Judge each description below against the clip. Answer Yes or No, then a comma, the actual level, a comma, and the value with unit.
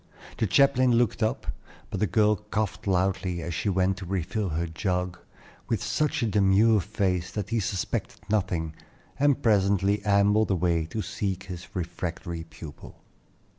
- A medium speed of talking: Yes, average, 150 wpm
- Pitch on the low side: Yes, very low, 95 Hz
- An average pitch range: Yes, average, 3.2 semitones